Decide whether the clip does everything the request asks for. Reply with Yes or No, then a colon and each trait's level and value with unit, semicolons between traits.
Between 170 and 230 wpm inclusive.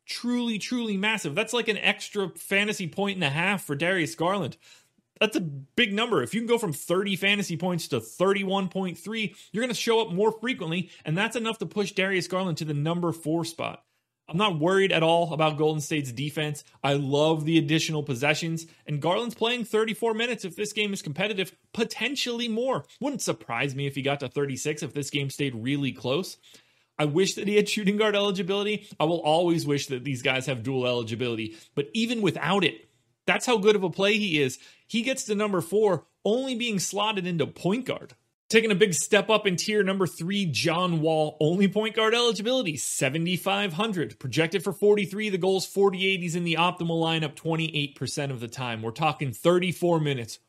Yes: fast, 205 wpm